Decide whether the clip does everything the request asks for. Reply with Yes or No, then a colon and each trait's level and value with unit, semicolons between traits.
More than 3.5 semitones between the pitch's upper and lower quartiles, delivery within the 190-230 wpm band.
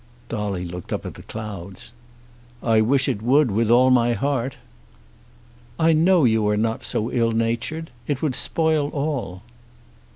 No: average, 4.5 semitones; average, 155 wpm